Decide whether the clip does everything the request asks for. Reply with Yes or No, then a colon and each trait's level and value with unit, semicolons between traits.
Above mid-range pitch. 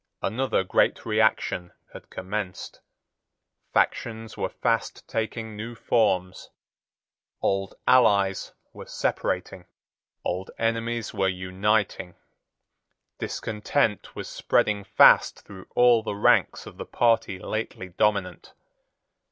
No: low, 105 Hz